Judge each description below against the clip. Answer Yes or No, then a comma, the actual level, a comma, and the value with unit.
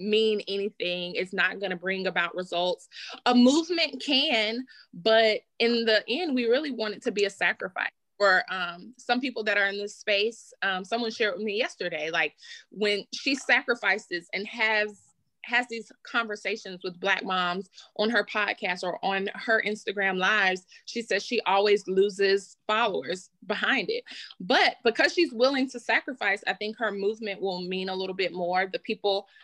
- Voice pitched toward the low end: No, high, 210 Hz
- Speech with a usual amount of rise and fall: Yes, average, 3.5 semitones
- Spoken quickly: No, average, 175 wpm